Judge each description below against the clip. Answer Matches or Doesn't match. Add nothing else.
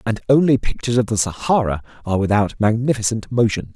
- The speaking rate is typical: Matches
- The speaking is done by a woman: Doesn't match